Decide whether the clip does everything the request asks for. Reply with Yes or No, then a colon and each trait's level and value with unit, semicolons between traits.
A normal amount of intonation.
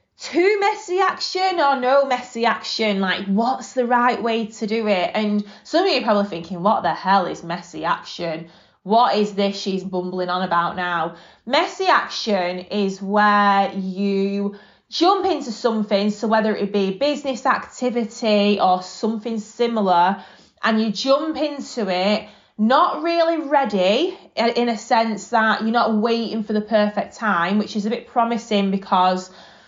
Yes: average, 3.8 semitones